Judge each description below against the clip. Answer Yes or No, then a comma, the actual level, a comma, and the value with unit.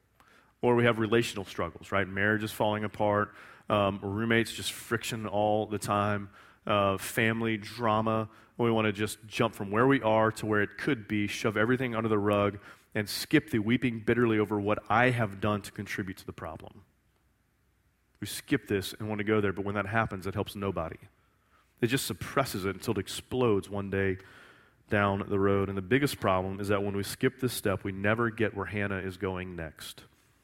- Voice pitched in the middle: No, low, 105 Hz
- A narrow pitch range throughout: Yes, narrow, 2.3 semitones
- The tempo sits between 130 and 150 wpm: No, average, 195 wpm